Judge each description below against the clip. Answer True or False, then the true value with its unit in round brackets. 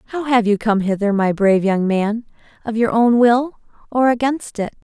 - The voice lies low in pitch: False (225 Hz)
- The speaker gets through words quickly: False (180 wpm)